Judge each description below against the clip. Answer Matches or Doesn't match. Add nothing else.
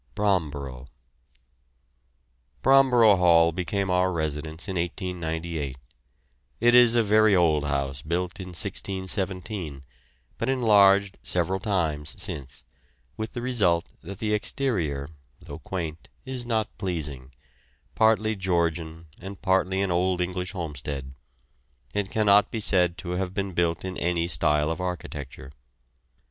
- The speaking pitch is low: Matches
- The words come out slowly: Matches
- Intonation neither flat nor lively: Matches